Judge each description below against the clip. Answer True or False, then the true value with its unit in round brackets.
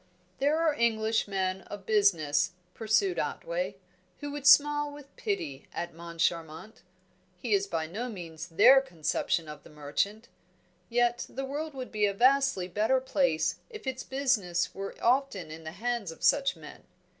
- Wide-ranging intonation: True (7.8 semitones)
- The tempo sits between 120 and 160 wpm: True (155 wpm)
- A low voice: False (220 Hz)